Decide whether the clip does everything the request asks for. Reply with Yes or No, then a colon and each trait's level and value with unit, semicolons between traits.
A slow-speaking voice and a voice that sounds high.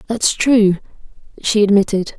Yes: slow, 110 wpm; high, 210 Hz